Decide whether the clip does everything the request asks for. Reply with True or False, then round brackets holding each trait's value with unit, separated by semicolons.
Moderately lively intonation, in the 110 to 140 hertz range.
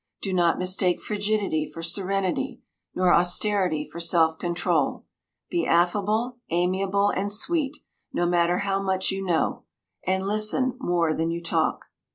False (3.0 semitones; 185 Hz)